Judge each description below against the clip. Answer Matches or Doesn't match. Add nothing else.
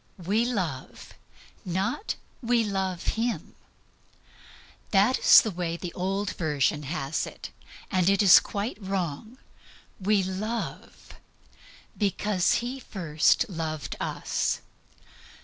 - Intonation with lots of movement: Doesn't match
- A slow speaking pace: Matches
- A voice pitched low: Doesn't match